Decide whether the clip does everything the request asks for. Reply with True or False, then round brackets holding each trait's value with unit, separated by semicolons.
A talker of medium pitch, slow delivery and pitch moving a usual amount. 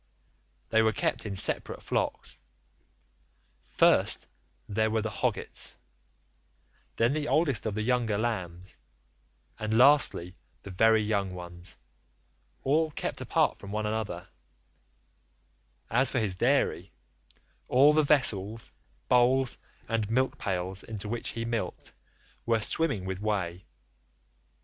False (110 Hz; 120 wpm; 4.1 semitones)